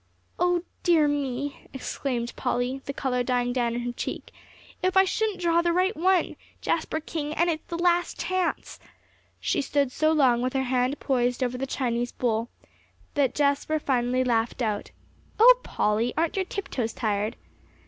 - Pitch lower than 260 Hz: No, very high, 270 Hz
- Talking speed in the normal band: Yes, average, 165 wpm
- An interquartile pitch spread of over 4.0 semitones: Yes, wide, 5.4 semitones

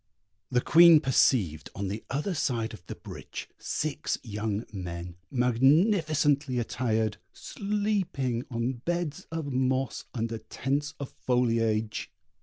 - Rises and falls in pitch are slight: No, average, 5.1 semitones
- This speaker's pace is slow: Yes, slow, 115 wpm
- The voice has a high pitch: No, low, 130 Hz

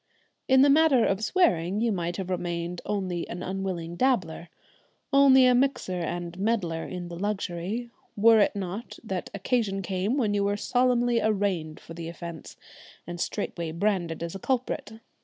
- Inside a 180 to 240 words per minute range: No, average, 160 wpm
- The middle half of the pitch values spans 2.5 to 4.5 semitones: No, average, 5.1 semitones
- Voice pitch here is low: No, high, 195 Hz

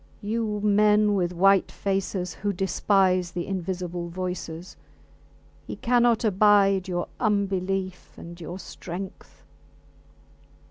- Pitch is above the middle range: Yes, high, 195 Hz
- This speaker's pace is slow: Yes, slow, 100 wpm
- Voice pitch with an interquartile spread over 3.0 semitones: No, narrow, 2.4 semitones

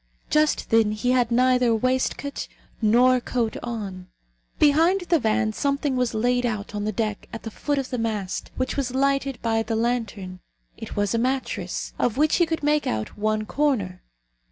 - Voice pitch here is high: Yes, high, 240 Hz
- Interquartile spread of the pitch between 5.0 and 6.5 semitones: No, average, 4.0 semitones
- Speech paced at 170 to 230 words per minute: Yes, average, 180 wpm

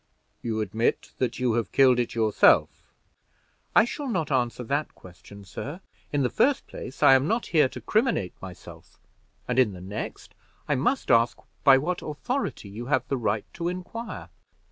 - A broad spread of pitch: Yes, wide, 6.7 semitones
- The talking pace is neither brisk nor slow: Yes, average, 170 wpm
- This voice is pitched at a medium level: No, low, 130 Hz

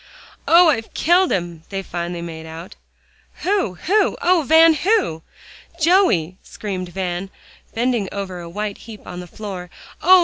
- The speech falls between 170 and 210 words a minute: No, average, 145 wpm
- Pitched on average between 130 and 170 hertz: No, high, 200 Hz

